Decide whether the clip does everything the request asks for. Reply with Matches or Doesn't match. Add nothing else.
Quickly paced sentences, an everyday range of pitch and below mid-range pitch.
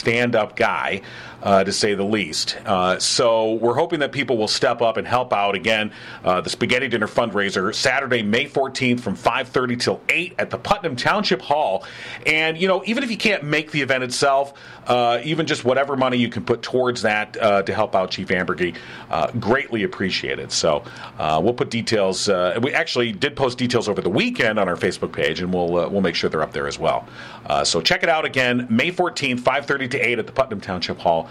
Doesn't match